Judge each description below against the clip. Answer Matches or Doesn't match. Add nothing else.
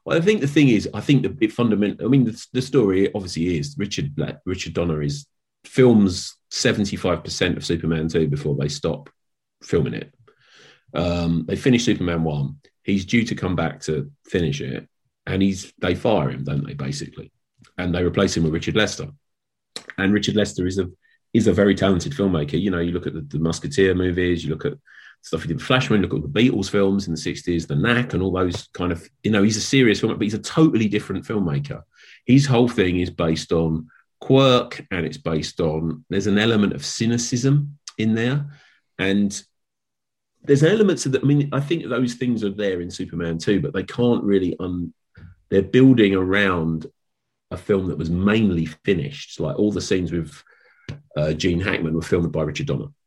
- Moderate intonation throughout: Doesn't match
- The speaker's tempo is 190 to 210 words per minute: Matches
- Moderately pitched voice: Doesn't match